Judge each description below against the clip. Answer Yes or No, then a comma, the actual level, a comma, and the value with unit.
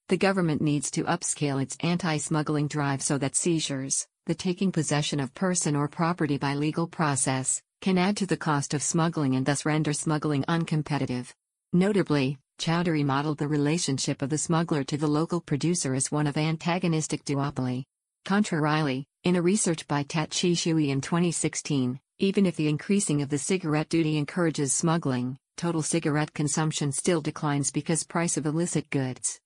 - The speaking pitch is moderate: Yes, medium, 155 Hz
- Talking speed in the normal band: Yes, average, 160 wpm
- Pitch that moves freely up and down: No, narrow, 2.6 semitones